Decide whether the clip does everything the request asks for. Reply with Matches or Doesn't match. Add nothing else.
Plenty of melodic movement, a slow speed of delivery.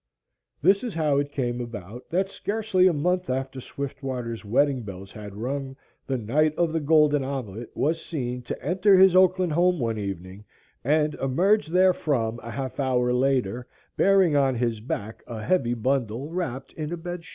Doesn't match